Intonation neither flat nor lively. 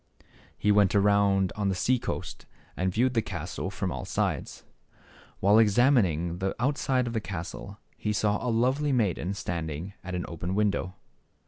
Yes: average, 3.9 semitones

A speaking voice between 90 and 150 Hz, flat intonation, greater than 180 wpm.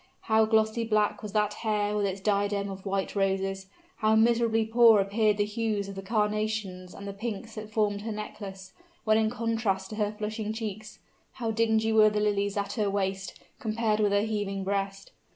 No: high, 210 Hz; narrow, 1.7 semitones; average, 190 wpm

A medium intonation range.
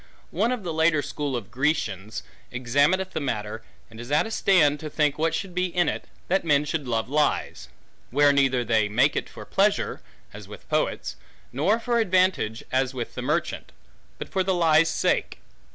No: wide, 6.2 semitones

